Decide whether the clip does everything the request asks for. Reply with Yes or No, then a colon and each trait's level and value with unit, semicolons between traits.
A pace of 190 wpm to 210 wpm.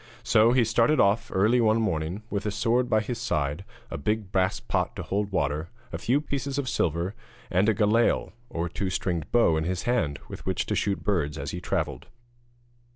Yes: average, 200 wpm